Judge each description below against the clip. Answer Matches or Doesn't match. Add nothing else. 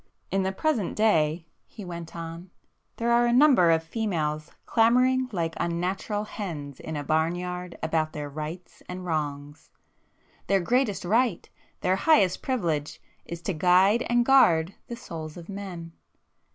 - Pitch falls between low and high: Matches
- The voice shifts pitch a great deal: Doesn't match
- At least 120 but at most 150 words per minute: Matches